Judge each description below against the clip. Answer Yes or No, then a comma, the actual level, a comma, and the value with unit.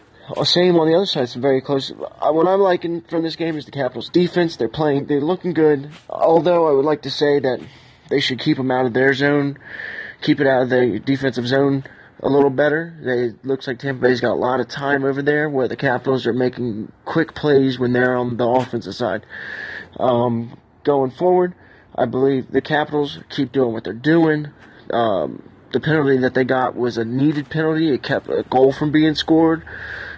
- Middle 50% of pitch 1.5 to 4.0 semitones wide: Yes, average, 3.4 semitones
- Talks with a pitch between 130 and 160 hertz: Yes, medium, 140 Hz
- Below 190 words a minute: No, fast, 205 wpm